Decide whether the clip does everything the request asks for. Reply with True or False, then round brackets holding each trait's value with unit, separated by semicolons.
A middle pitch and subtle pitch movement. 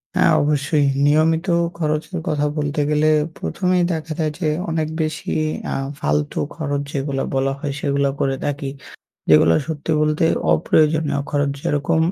True (150 Hz; 2.0 semitones)